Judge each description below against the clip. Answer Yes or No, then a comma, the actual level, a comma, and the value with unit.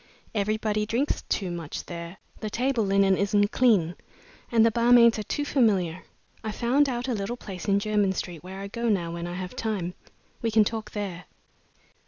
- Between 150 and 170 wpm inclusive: No, average, 185 wpm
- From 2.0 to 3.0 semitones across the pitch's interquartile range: No, average, 3.7 semitones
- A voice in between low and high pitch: No, high, 210 Hz